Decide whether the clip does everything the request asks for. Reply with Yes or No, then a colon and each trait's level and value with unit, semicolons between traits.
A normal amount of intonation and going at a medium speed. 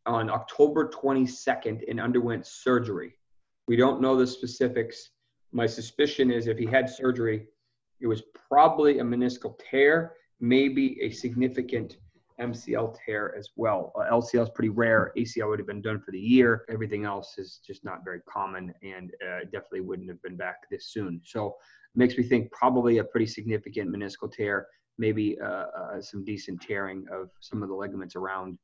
Yes: average, 3.1 semitones; average, 175 wpm